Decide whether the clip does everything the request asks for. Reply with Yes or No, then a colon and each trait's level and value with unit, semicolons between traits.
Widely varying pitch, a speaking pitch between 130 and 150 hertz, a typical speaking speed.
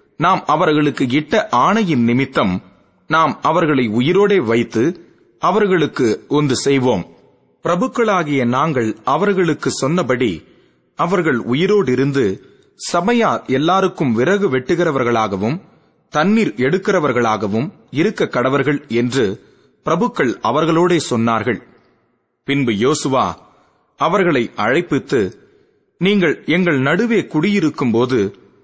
Yes: wide, 6.7 semitones; medium, 140 Hz; average, 85 wpm